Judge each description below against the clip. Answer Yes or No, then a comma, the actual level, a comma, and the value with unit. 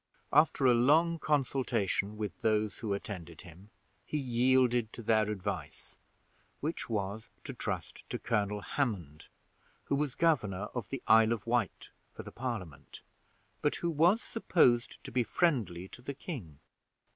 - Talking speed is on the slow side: No, average, 145 wpm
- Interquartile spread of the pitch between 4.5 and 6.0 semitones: Yes, average, 5.2 semitones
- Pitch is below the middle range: Yes, low, 115 Hz